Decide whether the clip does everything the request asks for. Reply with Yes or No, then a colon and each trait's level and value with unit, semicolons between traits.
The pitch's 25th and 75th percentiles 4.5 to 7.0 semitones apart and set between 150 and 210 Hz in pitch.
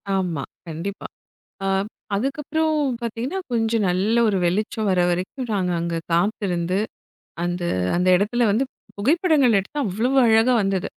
Yes: average, 4.8 semitones; high, 205 Hz